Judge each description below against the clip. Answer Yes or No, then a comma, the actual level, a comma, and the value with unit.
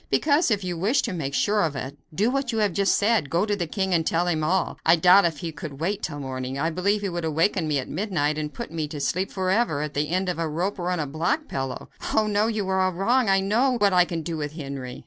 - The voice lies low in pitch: No, medium, 175 Hz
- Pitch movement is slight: No, average, 4.8 semitones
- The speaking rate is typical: No, fast, 280 wpm